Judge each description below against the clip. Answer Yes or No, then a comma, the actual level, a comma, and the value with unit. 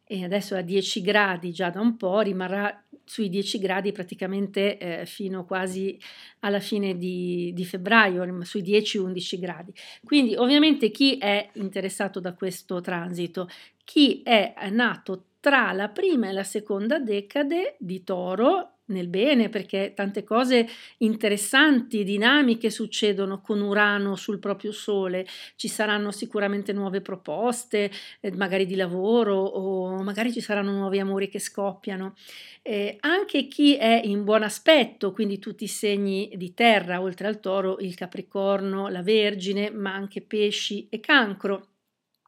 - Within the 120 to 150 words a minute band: Yes, average, 145 wpm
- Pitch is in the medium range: No, high, 205 Hz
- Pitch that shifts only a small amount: Yes, narrow, 2.2 semitones